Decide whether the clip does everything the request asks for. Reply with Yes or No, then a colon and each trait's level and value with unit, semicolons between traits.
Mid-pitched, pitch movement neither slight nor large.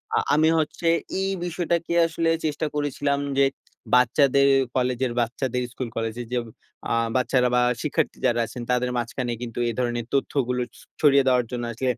No: low, 130 Hz; average, 3.0 semitones